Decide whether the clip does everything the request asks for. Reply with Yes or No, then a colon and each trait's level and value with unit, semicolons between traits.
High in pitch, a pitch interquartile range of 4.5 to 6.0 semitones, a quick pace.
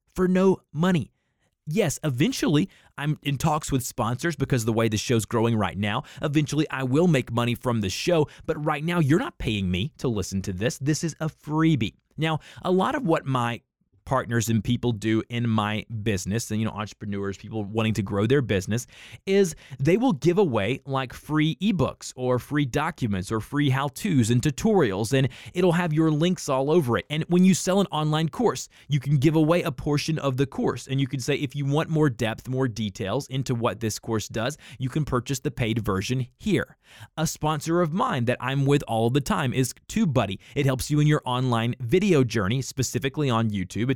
No: low, 135 Hz; average, 5.1 semitones; fast, 210 wpm